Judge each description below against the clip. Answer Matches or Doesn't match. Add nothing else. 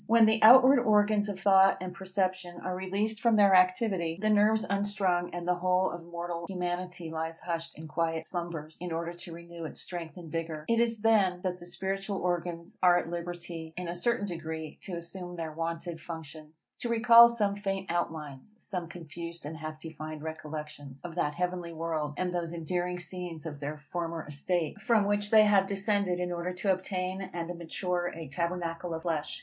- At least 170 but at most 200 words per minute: Matches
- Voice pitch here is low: Doesn't match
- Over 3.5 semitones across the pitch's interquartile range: Doesn't match